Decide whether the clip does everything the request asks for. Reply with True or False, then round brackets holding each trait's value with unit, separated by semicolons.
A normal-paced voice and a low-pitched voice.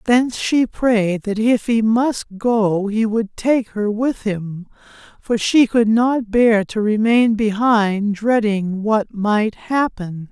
False (150 wpm; 220 Hz)